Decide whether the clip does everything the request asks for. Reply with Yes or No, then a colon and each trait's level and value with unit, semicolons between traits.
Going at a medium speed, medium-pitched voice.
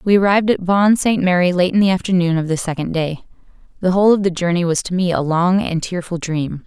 No: fast, 245 wpm; medium, 180 Hz